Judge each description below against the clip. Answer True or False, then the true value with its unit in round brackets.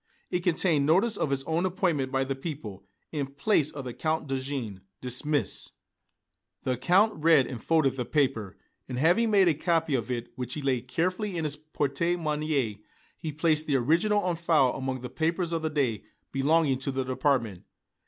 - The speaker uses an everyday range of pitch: True (4.0 semitones)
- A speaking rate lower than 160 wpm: False (185 wpm)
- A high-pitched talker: False (145 Hz)